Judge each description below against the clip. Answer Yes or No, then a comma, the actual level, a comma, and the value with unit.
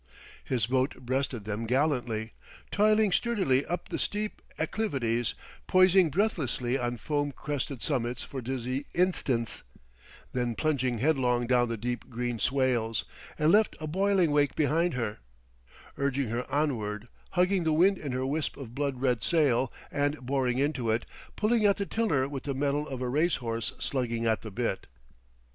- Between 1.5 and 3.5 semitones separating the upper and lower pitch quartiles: No, average, 4.4 semitones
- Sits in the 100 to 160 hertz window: Yes, low, 135 Hz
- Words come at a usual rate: Yes, average, 155 wpm